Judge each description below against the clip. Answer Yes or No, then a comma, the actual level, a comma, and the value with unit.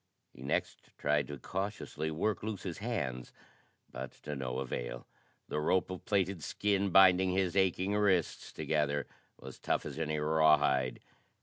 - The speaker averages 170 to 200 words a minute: No, average, 145 wpm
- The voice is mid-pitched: No, very low, 80 Hz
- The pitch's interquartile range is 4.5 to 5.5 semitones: Yes, average, 4.8 semitones